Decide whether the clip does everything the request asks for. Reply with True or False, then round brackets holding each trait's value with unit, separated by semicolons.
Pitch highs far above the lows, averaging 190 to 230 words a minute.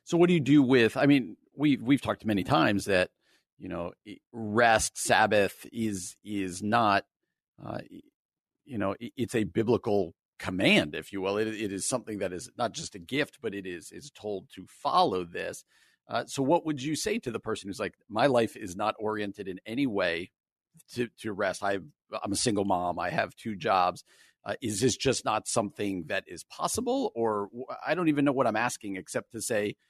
True (5.7 semitones; 200 wpm)